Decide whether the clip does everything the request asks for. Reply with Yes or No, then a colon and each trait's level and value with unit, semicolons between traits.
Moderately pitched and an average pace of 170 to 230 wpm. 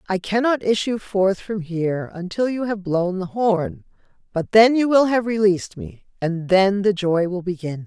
No: high, 195 Hz; average, 190 wpm